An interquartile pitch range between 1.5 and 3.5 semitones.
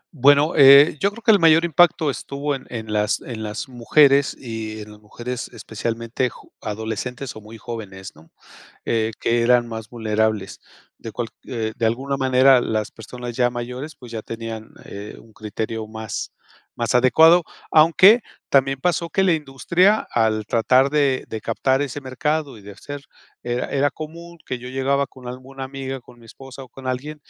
No: average, 3.9 semitones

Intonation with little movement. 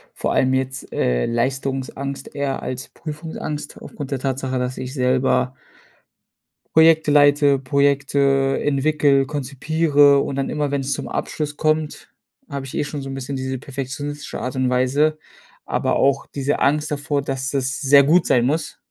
Yes: narrow, 1.8 semitones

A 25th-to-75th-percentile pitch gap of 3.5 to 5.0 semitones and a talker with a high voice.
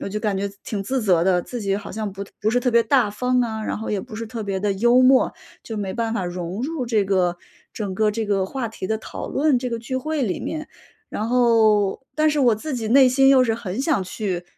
Yes: average, 3.9 semitones; high, 220 Hz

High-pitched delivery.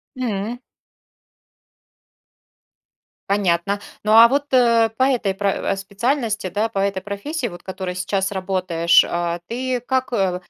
Yes: high, 200 Hz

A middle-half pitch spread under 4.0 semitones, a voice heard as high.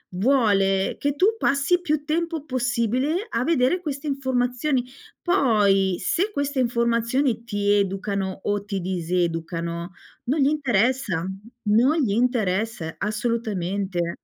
No: wide, 6.0 semitones; high, 235 Hz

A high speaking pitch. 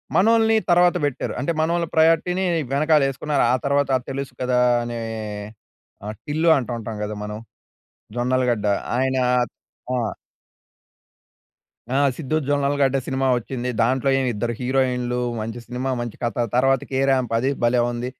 No: low, 130 Hz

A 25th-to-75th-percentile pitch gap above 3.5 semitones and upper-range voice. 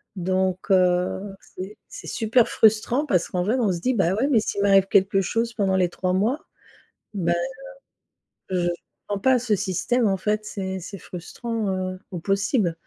No: average, 2.9 semitones; high, 195 Hz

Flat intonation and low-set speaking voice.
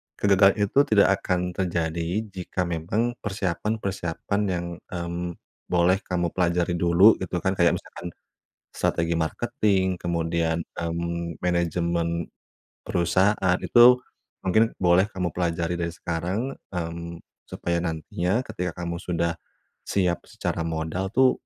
Yes: narrow, 2.0 semitones; very low, 90 Hz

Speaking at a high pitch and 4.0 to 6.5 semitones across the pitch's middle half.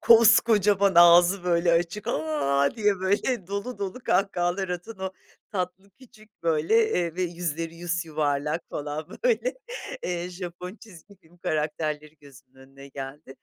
No: medium, 175 Hz; average, 4.3 semitones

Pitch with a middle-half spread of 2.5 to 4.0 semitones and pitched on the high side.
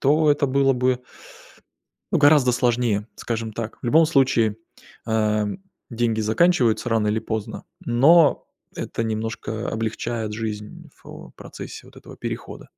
No: average, 3.4 semitones; low, 115 Hz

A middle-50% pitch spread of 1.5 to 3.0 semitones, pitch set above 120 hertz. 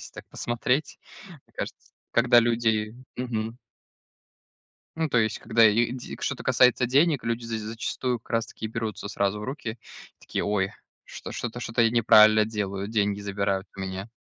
No: narrow, 2.4 semitones; low, 115 Hz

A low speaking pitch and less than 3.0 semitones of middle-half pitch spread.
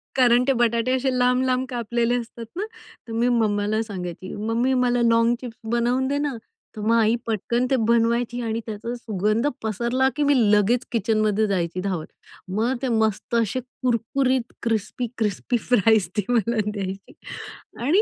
No: high, 230 Hz; narrow, 2.5 semitones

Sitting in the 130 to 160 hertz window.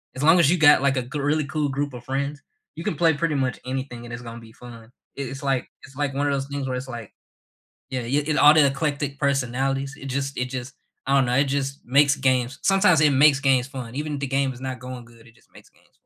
Yes: low, 135 Hz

